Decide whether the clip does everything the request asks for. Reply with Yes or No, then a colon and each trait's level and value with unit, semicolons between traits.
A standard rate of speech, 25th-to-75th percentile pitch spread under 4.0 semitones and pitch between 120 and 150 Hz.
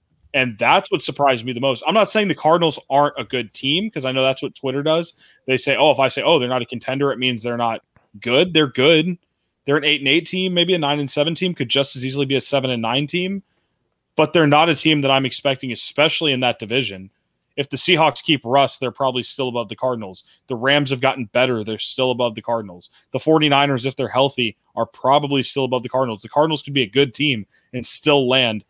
No: fast, 245 wpm; average, 2.8 semitones; low, 135 Hz